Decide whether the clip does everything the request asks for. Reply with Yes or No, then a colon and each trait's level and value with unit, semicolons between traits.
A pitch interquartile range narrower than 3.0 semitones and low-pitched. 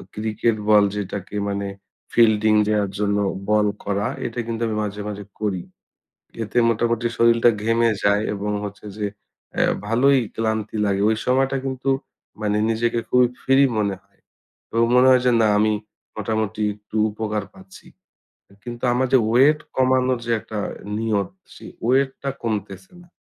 Yes: narrow, 2.6 semitones; low, 110 Hz